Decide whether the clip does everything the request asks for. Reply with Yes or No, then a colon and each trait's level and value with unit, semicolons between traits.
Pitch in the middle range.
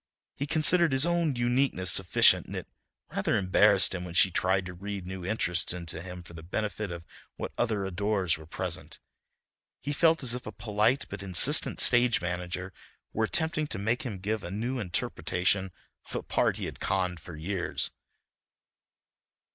No: very low, 95 Hz